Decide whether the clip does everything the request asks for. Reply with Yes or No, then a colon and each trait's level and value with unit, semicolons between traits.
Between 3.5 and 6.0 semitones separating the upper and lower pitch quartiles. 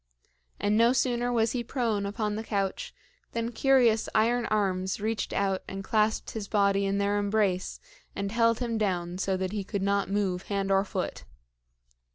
No: narrow, 2.6 semitones